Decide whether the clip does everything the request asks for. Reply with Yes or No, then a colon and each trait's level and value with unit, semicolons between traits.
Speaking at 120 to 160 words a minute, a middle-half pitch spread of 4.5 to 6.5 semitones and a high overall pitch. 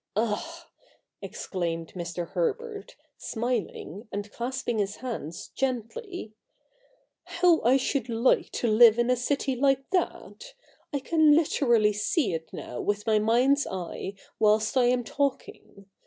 Yes: slow, 135 wpm; average, 5.0 semitones; high, 240 Hz